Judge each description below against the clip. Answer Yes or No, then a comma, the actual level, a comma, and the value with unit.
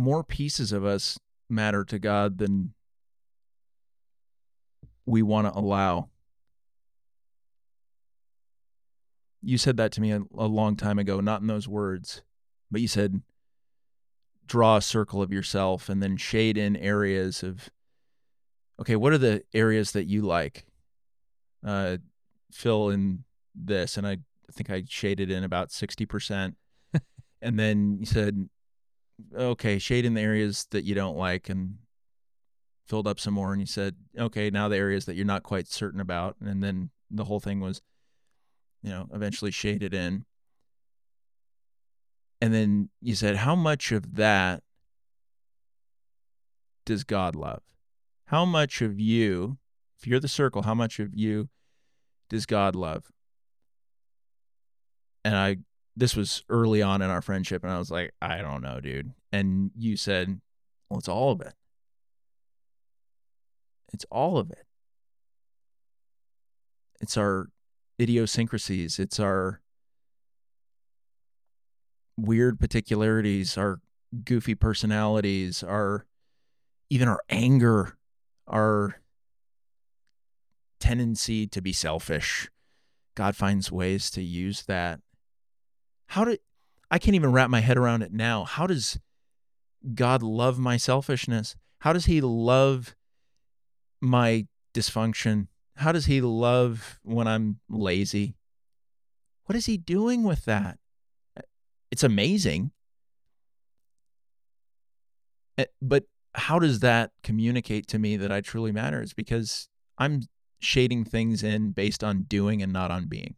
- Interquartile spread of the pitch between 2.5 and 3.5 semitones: Yes, average, 3.2 semitones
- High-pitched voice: No, low, 105 Hz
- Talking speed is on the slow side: Yes, slow, 130 wpm